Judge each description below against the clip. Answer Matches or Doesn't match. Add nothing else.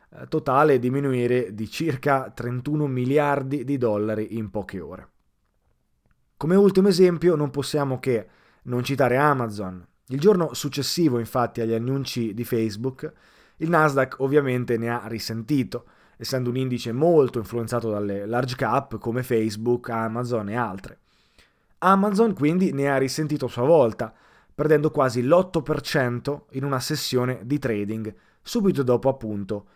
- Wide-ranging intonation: Doesn't match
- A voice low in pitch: Matches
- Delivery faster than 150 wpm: Doesn't match